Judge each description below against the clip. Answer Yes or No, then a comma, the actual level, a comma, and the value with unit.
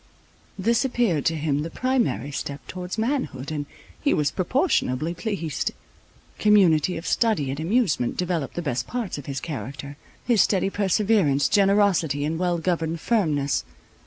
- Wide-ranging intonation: Yes, wide, 6.3 semitones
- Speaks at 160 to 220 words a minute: No, average, 145 wpm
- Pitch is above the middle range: No, medium, 170 Hz